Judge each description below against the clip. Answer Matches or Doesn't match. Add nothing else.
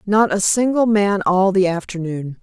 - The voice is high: Matches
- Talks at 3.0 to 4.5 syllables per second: Matches